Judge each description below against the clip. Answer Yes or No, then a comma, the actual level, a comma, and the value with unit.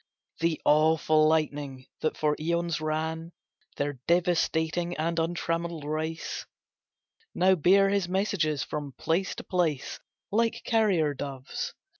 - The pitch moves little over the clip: Yes, narrow, 2.2 semitones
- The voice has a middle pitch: Yes, medium, 160 Hz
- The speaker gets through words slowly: Yes, slow, 115 wpm